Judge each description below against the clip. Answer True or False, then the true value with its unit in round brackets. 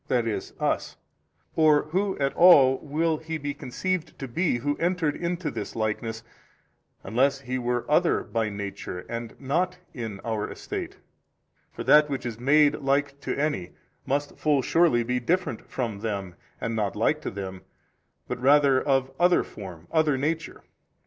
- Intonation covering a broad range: False (5.0 semitones)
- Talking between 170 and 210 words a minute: False (155 wpm)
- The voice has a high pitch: False (135 Hz)